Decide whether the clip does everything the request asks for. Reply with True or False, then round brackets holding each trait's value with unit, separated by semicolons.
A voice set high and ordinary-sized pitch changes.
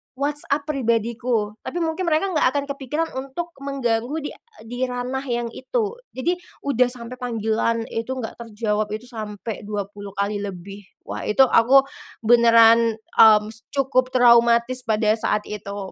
True (235 Hz; 3.6 semitones)